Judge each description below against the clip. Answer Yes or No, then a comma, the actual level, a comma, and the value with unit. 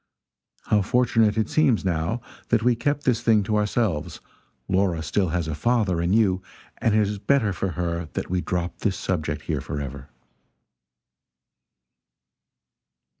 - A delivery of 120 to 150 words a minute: Yes, average, 145 wpm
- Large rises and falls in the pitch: No, average, 4.7 semitones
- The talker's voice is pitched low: Yes, low, 100 Hz